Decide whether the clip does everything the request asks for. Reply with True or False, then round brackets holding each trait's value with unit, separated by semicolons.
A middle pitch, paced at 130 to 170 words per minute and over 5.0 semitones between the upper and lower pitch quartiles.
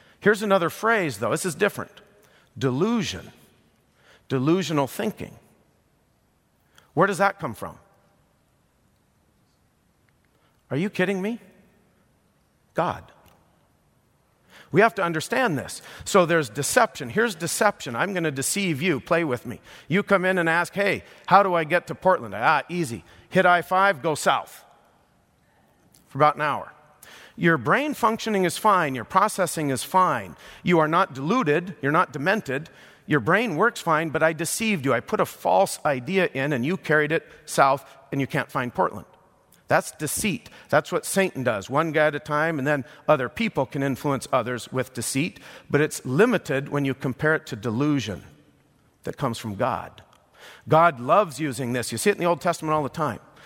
True (155 Hz; 165 wpm; 5.5 semitones)